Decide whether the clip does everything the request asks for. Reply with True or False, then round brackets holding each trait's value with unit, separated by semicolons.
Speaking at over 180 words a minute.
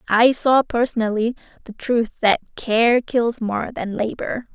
False (145 wpm)